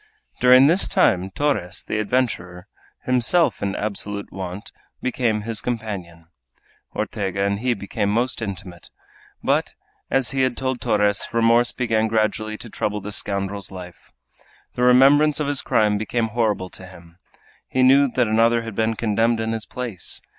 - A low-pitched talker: Yes, low, 110 Hz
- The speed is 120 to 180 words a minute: Yes, average, 155 wpm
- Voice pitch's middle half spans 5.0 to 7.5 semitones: No, average, 3.7 semitones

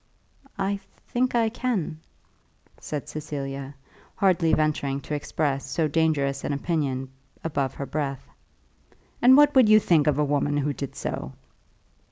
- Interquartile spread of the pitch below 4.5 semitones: No, average, 4.8 semitones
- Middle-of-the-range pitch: Yes, medium, 150 Hz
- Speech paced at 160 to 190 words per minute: No, average, 140 wpm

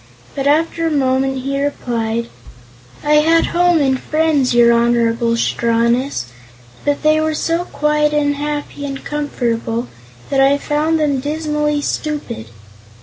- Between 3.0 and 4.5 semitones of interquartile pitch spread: Yes, average, 3.7 semitones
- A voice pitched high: Yes, very high, 285 Hz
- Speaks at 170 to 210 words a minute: No, slow, 135 wpm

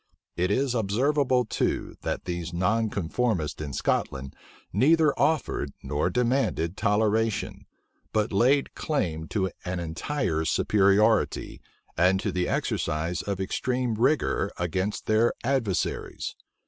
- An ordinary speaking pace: No, slow, 110 wpm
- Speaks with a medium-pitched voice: No, low, 105 Hz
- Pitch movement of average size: No, wide, 6.0 semitones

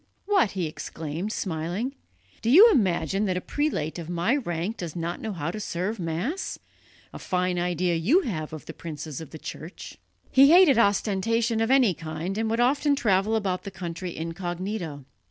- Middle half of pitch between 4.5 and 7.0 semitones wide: Yes, average, 5.3 semitones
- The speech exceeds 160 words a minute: Yes, average, 175 wpm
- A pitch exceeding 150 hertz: Yes, medium, 185 Hz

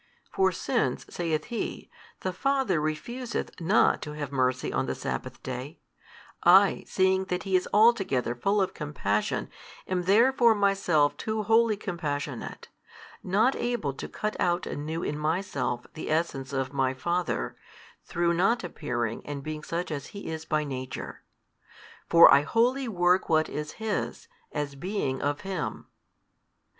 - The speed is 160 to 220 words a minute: No, average, 145 wpm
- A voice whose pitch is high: No, medium, 170 Hz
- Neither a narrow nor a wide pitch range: No, wide, 5.7 semitones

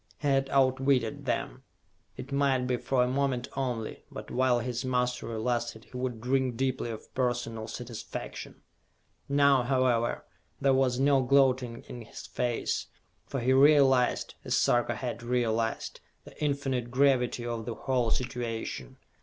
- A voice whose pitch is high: No, low, 125 Hz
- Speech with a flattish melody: Yes, narrow, 2.0 semitones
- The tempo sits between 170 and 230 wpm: No, average, 145 wpm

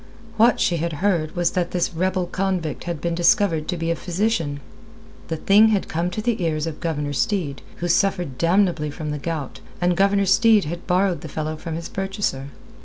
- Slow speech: No, average, 195 wpm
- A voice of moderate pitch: Yes, medium, 175 Hz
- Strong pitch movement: No, average, 3.5 semitones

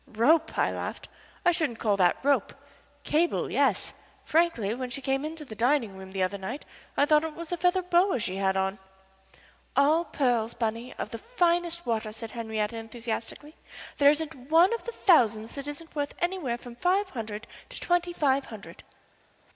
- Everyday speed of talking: Yes, average, 180 wpm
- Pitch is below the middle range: No, very high, 270 Hz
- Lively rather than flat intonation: Yes, wide, 6.7 semitones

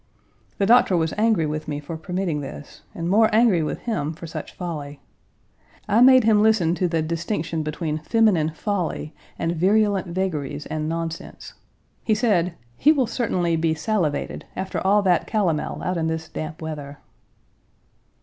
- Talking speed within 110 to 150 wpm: No, average, 160 wpm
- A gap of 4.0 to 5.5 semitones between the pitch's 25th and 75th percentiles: Yes, average, 4.7 semitones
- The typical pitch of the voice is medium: Yes, medium, 170 Hz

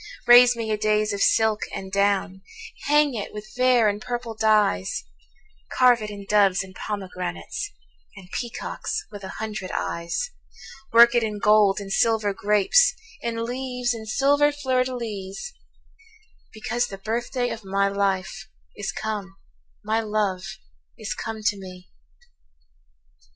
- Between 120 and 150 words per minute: Yes, average, 140 wpm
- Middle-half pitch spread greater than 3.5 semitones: No, average, 3.2 semitones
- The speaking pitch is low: No, high, 215 Hz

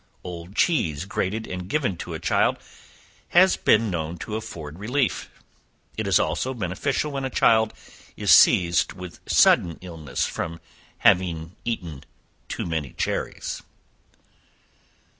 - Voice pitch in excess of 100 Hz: No, very low, 90 Hz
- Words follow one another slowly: Yes, slow, 125 wpm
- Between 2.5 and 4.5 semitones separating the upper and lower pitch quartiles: No, average, 5.2 semitones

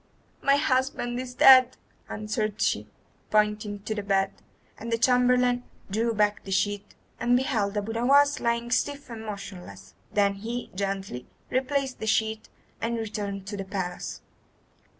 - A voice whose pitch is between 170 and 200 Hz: No, high, 220 Hz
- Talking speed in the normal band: Yes, average, 145 wpm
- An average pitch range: Yes, average, 3.4 semitones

